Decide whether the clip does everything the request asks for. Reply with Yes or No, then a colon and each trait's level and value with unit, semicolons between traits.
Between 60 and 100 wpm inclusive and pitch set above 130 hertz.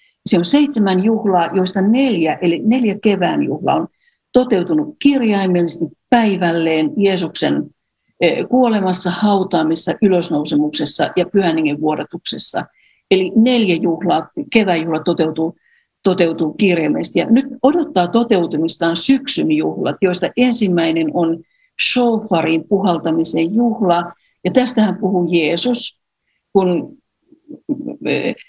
Yes: slow, 95 wpm; high, 190 Hz